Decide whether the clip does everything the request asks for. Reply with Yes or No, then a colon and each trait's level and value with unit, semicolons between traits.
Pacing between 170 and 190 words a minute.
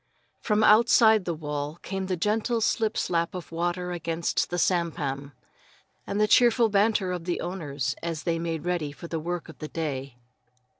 Yes: average, 180 wpm